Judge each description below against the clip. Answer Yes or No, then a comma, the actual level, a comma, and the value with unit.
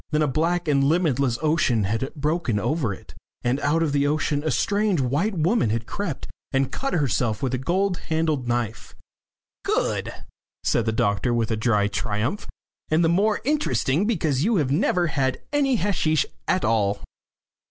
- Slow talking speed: No, average, 165 wpm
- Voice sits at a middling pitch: Yes, medium, 145 Hz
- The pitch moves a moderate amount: No, wide, 6.1 semitones